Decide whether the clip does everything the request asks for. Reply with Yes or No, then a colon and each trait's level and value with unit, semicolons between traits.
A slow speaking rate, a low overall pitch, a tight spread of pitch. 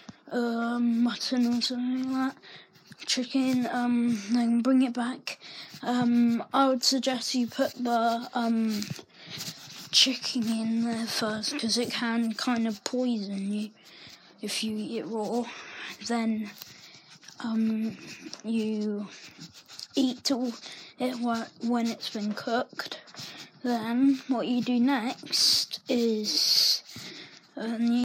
No: slow, 110 wpm; high, 235 Hz; narrow, 2.1 semitones